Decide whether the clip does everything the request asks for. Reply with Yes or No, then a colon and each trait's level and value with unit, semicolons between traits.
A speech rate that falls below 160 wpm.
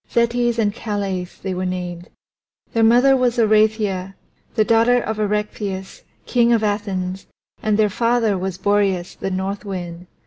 Yes: average, 145 wpm